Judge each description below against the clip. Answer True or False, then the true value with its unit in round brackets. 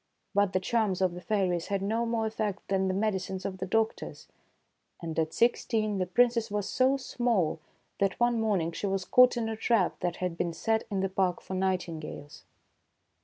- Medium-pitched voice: False (195 Hz)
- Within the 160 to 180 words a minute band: False (190 wpm)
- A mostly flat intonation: False (3.4 semitones)